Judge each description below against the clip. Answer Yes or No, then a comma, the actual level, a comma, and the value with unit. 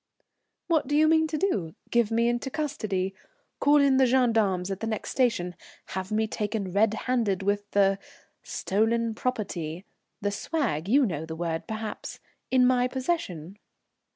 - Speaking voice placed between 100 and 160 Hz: No, high, 220 Hz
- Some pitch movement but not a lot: Yes, average, 4.9 semitones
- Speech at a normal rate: Yes, average, 155 wpm